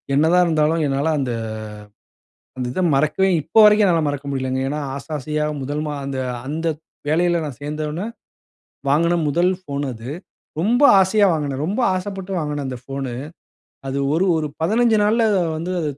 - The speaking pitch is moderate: Yes, medium, 155 Hz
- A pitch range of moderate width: Yes, average, 4.3 semitones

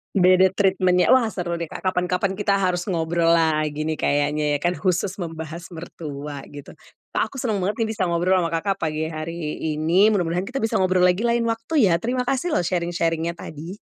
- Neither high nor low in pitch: Yes, medium, 175 Hz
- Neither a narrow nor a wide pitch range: Yes, average, 3.0 semitones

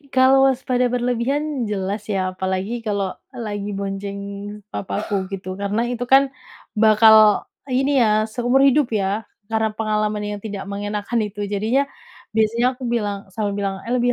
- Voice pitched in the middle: No, high, 215 Hz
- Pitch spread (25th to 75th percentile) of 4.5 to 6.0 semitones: No, average, 3.3 semitones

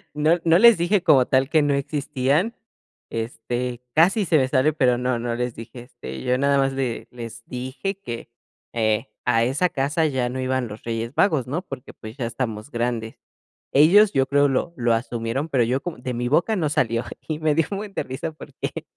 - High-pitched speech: No, low, 130 Hz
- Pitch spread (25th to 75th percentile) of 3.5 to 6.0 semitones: Yes, average, 4.5 semitones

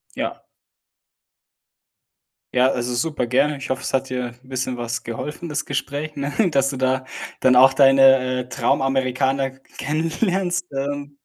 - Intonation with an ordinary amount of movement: No, narrow, 2.1 semitones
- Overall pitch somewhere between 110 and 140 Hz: Yes, low, 135 Hz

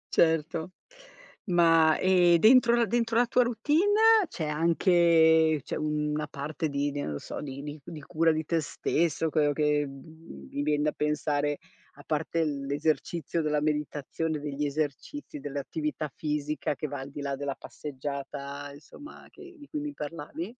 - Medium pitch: Yes, medium, 155 Hz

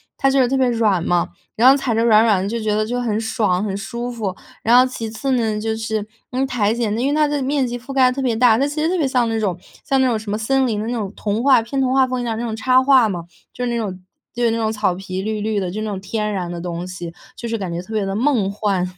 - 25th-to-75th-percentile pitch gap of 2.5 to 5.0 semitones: Yes, average, 3.5 semitones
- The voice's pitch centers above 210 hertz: Yes, high, 225 Hz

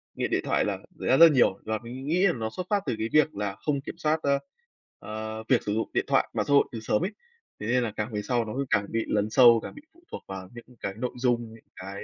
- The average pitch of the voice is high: No, low, 115 Hz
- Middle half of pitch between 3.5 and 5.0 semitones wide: Yes, average, 4.5 semitones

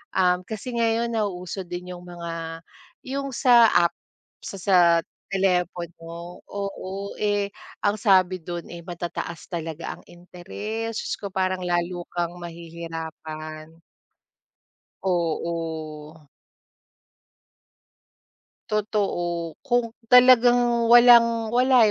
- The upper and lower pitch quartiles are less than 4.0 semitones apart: No, average, 4.7 semitones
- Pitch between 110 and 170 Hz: No, medium, 180 Hz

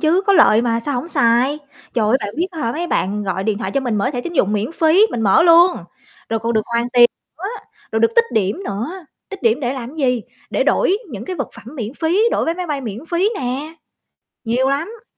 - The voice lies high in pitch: Yes, very high, 255 Hz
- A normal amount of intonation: No, wide, 6.5 semitones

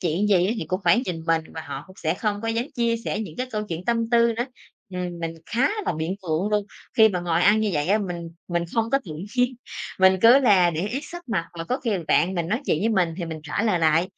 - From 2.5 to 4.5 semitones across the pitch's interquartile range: No, average, 5.2 semitones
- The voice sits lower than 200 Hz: Yes, high, 190 Hz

